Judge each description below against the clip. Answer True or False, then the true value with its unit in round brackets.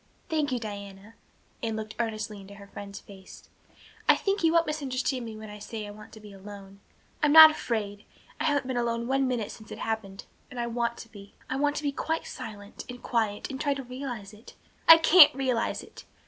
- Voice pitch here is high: True (230 Hz)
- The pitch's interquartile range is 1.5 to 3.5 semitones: False (4.7 semitones)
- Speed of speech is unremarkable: False (215 wpm)